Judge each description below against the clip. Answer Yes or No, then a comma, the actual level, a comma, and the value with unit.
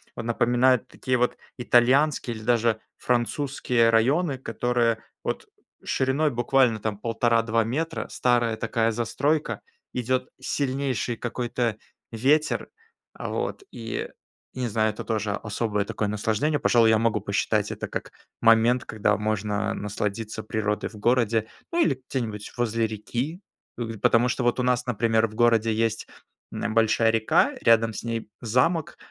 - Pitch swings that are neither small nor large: No, narrow, 2.3 semitones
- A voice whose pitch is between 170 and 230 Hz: No, low, 115 Hz